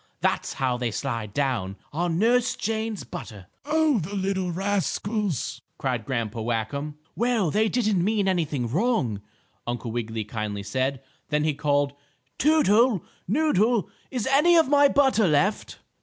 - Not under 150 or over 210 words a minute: No, average, 140 wpm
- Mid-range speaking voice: Yes, medium, 175 Hz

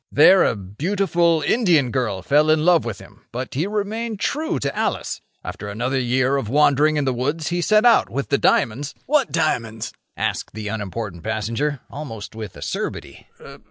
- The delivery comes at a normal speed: Yes, average, 170 wpm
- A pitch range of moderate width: No, wide, 7.0 semitones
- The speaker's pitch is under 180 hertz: Yes, medium, 140 Hz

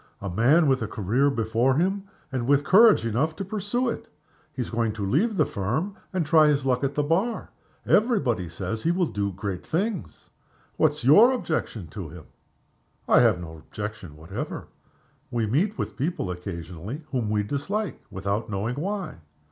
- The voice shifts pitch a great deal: Yes, wide, 8.9 semitones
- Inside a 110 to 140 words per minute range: No, average, 175 wpm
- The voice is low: Yes, low, 130 Hz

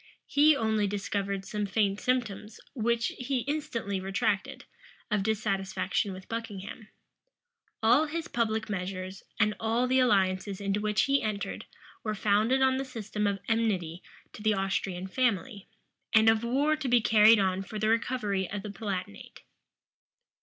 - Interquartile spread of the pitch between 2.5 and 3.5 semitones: Yes, average, 3.2 semitones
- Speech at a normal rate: Yes, average, 145 wpm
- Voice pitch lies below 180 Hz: No, high, 215 Hz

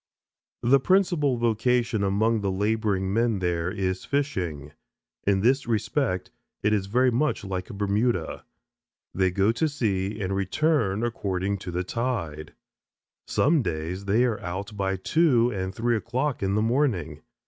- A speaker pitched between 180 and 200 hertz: No, low, 105 Hz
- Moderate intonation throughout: Yes, average, 4.4 semitones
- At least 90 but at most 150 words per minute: Yes, average, 145 wpm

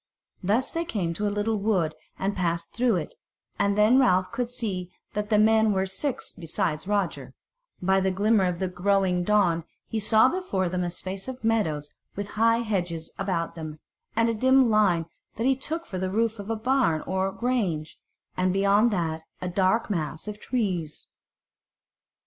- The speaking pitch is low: No, high, 200 Hz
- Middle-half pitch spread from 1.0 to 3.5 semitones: No, average, 3.9 semitones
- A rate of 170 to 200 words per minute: Yes, average, 180 wpm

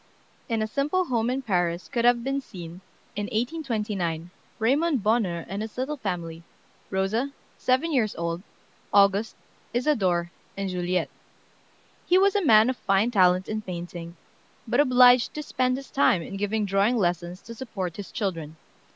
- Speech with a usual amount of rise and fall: No, wide, 5.7 semitones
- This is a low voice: No, high, 215 Hz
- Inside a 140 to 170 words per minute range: Yes, average, 160 wpm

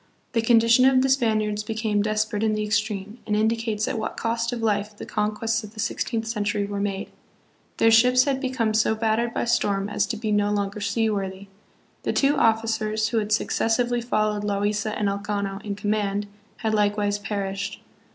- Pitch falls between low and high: No, high, 215 Hz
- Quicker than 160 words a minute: Yes, average, 185 wpm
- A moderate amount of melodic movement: No, narrow, 1.7 semitones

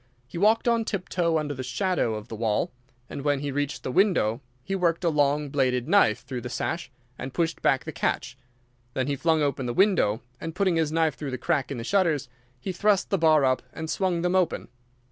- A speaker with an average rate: No, fast, 220 wpm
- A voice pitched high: No, medium, 150 Hz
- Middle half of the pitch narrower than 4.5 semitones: No, average, 5.2 semitones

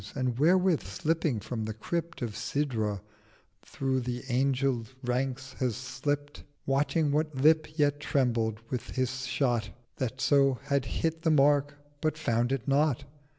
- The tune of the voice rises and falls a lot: No, average, 3.1 semitones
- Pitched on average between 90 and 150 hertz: Yes, low, 135 Hz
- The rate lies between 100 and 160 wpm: Yes, average, 140 wpm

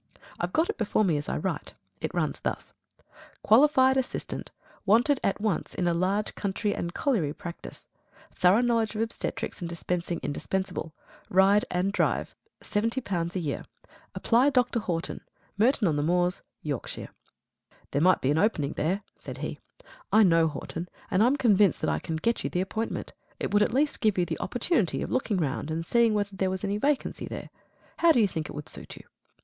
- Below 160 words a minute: No, average, 190 wpm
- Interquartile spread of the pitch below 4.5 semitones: No, average, 4.9 semitones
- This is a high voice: Yes, high, 195 Hz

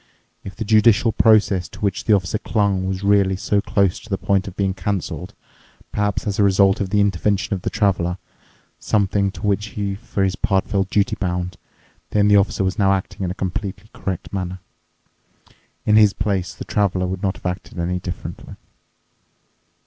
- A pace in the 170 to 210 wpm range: Yes, average, 180 wpm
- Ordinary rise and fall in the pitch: No, narrow, 1.6 semitones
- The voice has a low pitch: Yes, low, 100 Hz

